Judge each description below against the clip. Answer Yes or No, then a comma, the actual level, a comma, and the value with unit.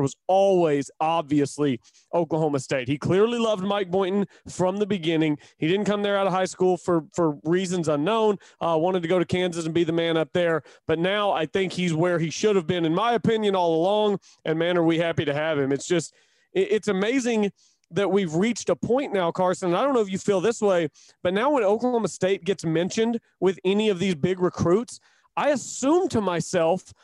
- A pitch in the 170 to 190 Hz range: Yes, medium, 185 Hz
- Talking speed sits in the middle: No, fast, 220 wpm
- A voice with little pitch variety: No, average, 3.5 semitones